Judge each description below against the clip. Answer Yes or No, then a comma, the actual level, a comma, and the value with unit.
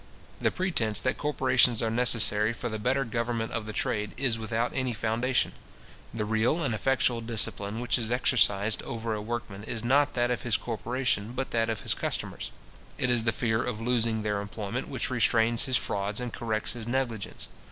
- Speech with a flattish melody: Yes, narrow, 2.2 semitones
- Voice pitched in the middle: No, low, 115 Hz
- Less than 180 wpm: No, average, 185 wpm